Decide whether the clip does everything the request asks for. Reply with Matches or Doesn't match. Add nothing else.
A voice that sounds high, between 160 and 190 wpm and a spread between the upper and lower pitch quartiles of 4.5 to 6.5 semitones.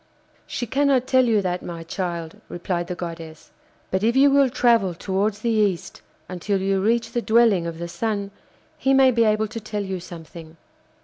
Matches